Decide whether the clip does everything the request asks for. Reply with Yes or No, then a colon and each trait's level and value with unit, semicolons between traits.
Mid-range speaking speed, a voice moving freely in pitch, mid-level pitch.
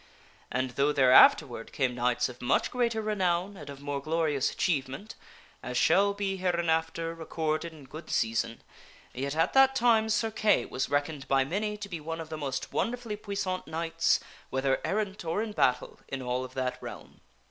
Yes: average, 180 wpm; wide, 6.8 semitones; medium, 160 Hz